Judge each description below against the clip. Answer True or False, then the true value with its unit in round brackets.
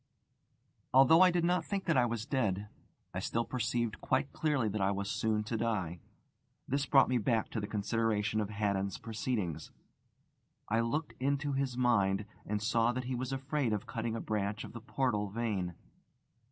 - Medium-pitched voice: False (115 Hz)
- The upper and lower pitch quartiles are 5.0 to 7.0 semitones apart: False (3.8 semitones)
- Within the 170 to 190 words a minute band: True (180 wpm)